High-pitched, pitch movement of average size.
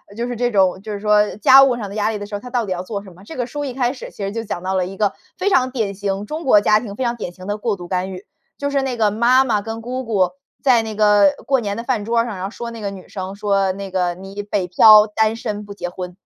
Yes: high, 210 Hz; average, 3.3 semitones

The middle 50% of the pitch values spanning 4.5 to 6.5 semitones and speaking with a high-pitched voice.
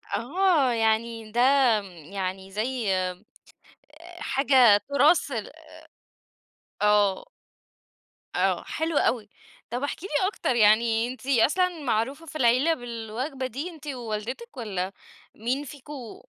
Yes: average, 4.9 semitones; high, 245 Hz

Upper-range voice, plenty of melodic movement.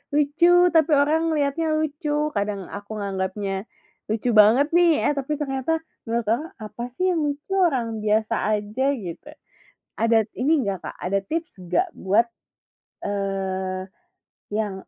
Yes: high, 230 Hz; wide, 6.6 semitones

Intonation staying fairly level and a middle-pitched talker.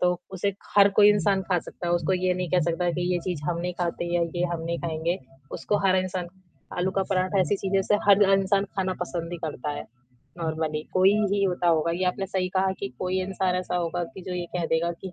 Yes: narrow, 1.8 semitones; medium, 180 Hz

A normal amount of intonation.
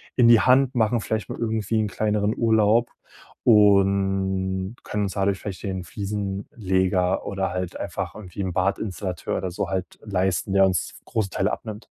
No: narrow, 2.3 semitones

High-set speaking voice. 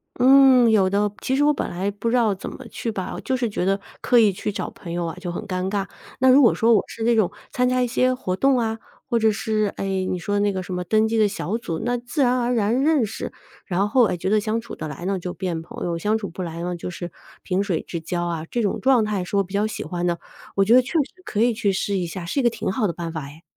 Yes: high, 205 Hz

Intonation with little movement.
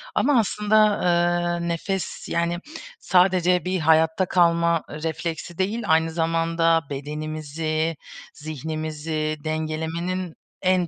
Yes: narrow, 2.2 semitones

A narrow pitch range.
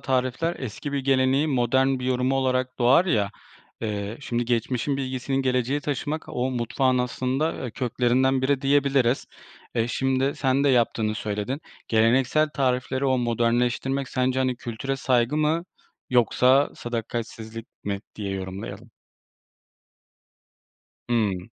Yes: narrow, 2.3 semitones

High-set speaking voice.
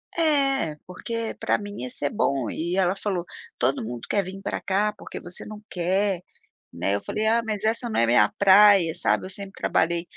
Yes: high, 195 Hz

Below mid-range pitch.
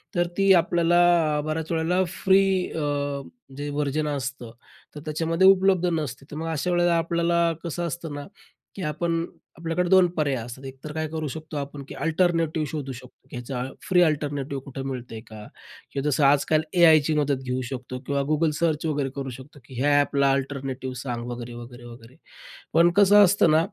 No: medium, 150 Hz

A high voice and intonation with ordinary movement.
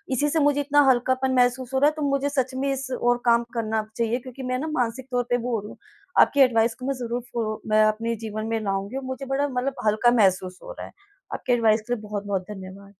Yes: high, 245 Hz; average, 3.5 semitones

